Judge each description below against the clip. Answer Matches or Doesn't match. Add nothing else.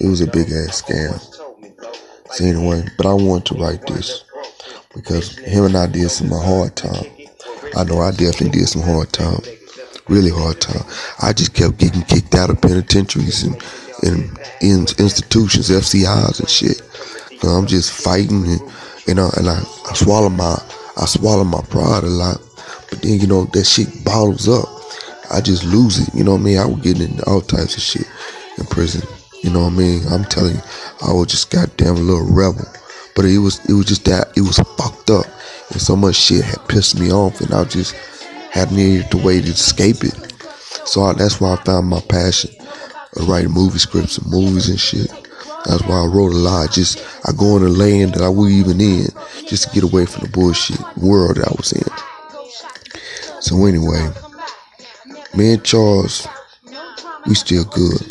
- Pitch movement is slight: Matches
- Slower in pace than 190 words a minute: Doesn't match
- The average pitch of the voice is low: Matches